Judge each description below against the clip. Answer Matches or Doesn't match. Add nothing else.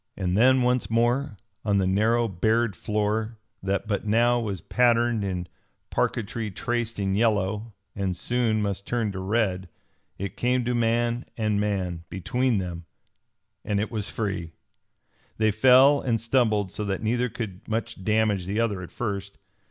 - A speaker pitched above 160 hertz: Doesn't match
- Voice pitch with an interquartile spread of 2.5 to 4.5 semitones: Matches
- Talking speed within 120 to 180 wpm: Matches